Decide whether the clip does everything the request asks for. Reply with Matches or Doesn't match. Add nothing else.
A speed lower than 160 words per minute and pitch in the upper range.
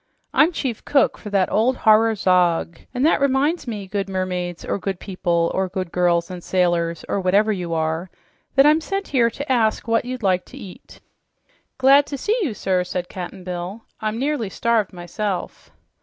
Doesn't match